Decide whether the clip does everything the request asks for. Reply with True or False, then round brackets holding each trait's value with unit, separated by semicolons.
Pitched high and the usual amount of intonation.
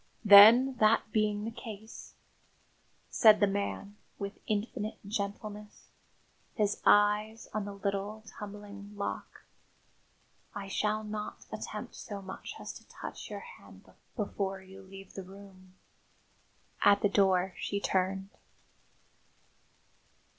False (205 Hz; 1.4 semitones)